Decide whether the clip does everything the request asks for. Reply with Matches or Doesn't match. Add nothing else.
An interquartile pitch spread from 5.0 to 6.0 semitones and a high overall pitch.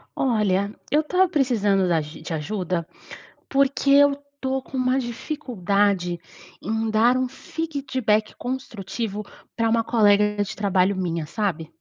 Matches